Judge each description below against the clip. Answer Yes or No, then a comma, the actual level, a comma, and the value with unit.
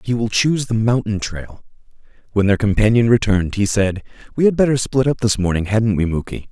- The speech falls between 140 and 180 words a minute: No, fast, 205 wpm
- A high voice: No, low, 110 Hz